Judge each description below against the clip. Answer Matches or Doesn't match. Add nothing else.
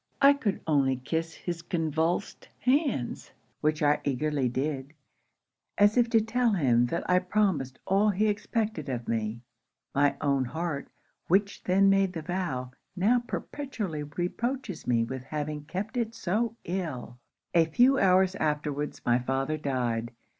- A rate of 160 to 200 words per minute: Doesn't match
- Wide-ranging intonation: Matches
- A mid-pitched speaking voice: Matches